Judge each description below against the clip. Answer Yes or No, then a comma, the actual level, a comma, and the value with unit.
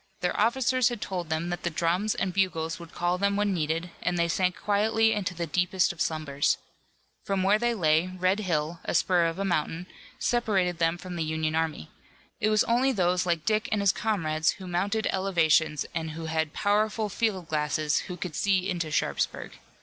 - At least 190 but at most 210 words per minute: Yes, average, 195 wpm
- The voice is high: No, medium, 180 Hz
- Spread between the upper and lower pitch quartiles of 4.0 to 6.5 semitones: No, average, 3.6 semitones